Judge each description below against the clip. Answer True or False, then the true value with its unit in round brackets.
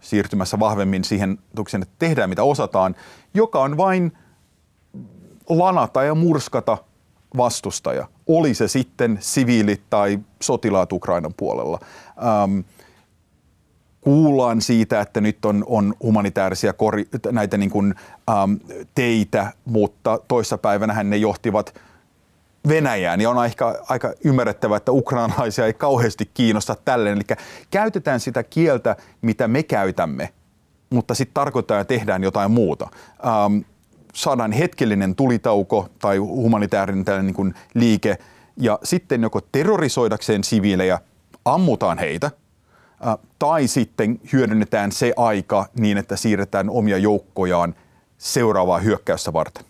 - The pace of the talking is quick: False (105 wpm)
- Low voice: True (110 Hz)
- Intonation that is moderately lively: True (3.8 semitones)